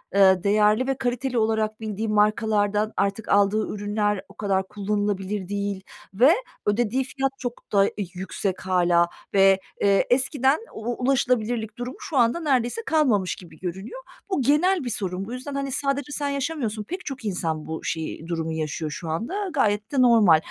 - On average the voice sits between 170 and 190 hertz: No, high, 215 Hz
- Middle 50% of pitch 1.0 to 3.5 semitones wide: No, average, 4.7 semitones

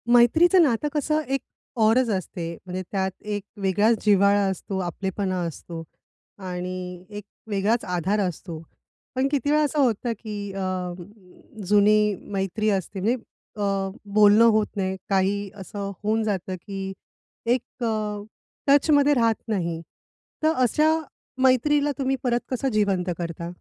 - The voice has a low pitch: No, high, 205 Hz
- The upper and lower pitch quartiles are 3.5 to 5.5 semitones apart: Yes, average, 4.1 semitones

